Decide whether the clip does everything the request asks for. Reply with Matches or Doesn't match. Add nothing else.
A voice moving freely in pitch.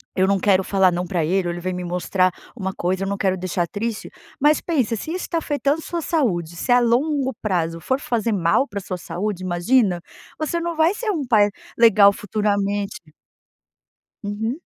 Matches